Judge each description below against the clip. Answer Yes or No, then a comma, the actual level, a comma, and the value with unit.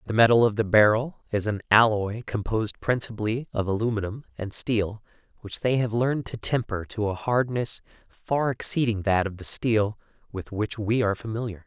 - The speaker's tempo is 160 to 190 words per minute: Yes, average, 175 wpm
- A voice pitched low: Yes, low, 110 Hz